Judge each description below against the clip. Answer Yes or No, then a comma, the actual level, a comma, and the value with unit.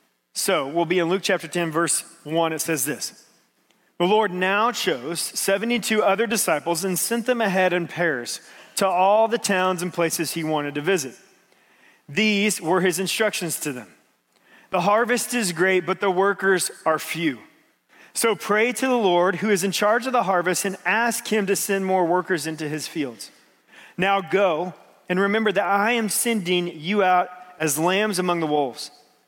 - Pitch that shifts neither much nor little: Yes, average, 3.4 semitones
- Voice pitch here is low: No, medium, 185 Hz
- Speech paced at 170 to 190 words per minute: Yes, average, 180 wpm